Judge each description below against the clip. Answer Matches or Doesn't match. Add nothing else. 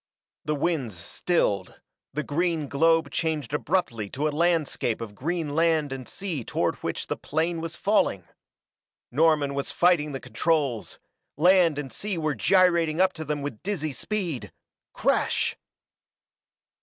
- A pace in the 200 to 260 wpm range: Doesn't match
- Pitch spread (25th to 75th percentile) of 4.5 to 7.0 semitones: Doesn't match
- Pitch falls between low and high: Matches